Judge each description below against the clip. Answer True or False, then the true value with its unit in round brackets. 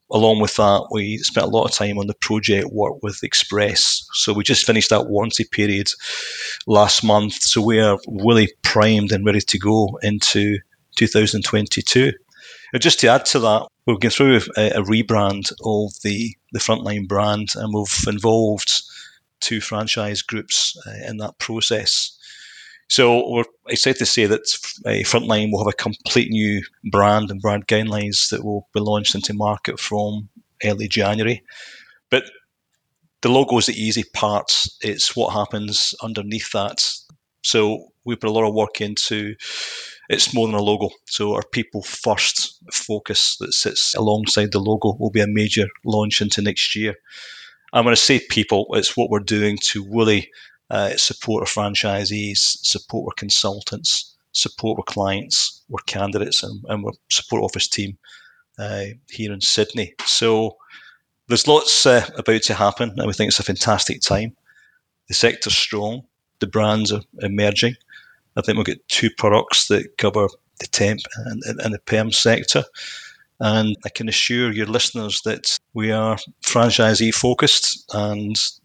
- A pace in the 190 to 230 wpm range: False (160 wpm)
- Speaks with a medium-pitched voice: False (105 Hz)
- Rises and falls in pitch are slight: True (1.4 semitones)